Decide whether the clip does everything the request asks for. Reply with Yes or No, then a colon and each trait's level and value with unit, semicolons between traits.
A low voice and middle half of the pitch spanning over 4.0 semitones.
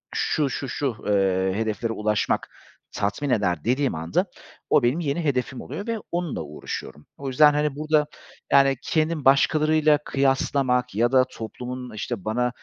Yes: low, 130 Hz; average, 5.2 semitones